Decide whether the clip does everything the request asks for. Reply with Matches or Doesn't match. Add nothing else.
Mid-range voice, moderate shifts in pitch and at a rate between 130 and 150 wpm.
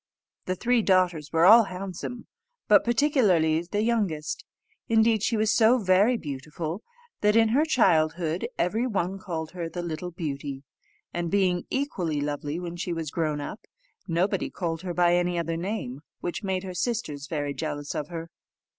Doesn't match